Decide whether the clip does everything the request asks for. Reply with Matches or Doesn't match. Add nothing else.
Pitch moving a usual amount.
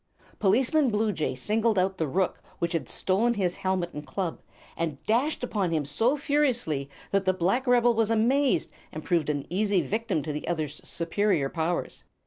Doesn't match